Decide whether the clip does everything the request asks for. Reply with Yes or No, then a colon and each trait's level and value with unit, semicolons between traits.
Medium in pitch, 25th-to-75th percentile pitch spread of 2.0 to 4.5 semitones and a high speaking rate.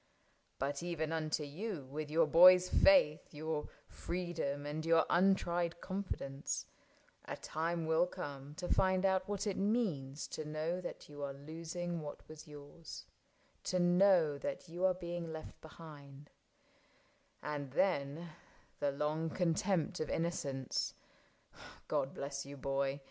No: medium, 160 Hz; average, 3.5 semitones; average, 140 wpm